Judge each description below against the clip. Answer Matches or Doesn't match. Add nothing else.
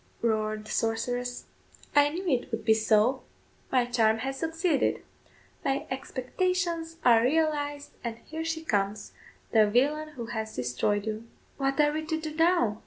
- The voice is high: Matches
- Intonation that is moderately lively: Doesn't match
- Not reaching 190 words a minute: Matches